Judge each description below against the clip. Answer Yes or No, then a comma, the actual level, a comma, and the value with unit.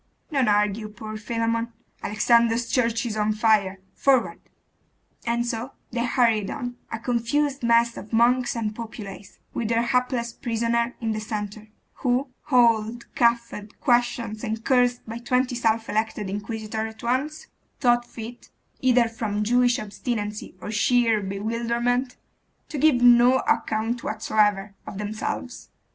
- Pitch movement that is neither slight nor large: No, narrow, 2.2 semitones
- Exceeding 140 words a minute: No, slow, 135 wpm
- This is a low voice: No, high, 230 Hz